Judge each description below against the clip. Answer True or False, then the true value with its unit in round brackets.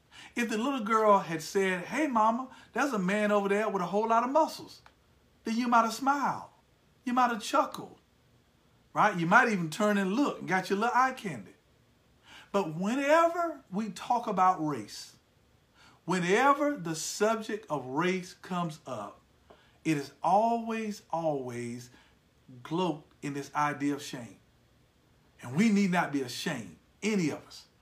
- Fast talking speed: False (155 wpm)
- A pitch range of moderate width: False (6.2 semitones)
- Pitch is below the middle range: False (200 Hz)